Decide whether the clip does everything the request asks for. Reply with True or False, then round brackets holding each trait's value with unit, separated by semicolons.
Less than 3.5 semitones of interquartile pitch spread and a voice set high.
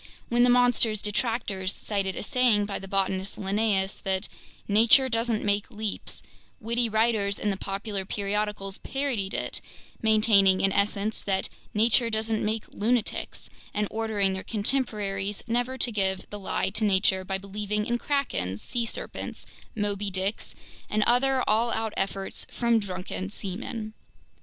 True (2.7 semitones; 210 Hz)